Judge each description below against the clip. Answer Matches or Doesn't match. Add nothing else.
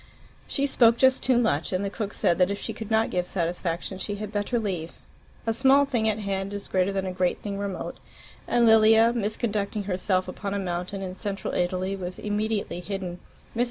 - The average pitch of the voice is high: Matches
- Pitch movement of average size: Matches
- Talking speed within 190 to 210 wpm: Matches